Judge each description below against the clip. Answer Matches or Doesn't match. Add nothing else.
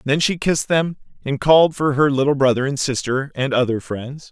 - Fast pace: Matches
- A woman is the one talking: Doesn't match